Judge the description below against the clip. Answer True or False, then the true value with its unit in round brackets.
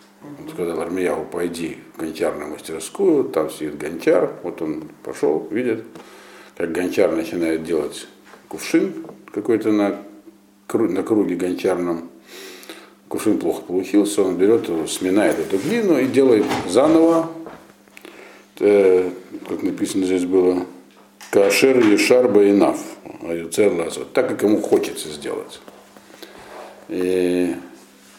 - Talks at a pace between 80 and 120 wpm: True (110 wpm)